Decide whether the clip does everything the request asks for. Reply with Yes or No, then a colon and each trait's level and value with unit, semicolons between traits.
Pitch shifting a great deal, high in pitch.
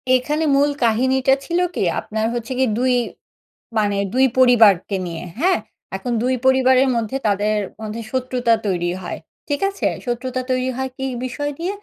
No: average, 3.2 semitones; very high, 255 Hz